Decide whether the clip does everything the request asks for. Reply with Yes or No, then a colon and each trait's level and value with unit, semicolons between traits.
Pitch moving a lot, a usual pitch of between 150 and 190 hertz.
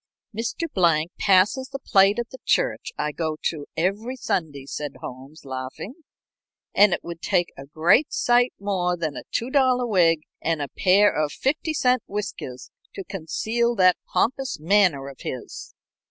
Yes: wide, 7.3 semitones; medium, 185 Hz